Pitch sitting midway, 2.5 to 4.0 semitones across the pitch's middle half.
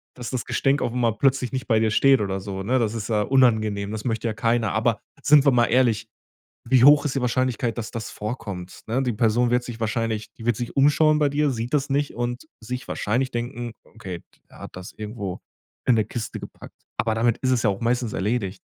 No: low, 120 Hz; average, 2.9 semitones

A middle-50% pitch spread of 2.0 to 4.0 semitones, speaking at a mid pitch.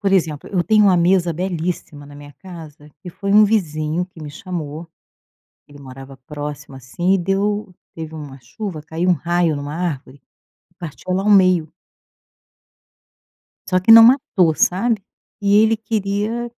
No: average, 4.6 semitones; medium, 175 Hz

